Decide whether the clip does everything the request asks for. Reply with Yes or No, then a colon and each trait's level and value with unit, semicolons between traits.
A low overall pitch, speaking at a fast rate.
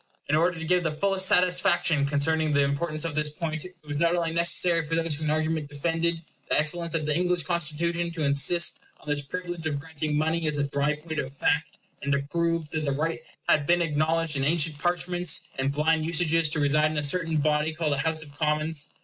No: medium, 155 Hz; fast, 220 wpm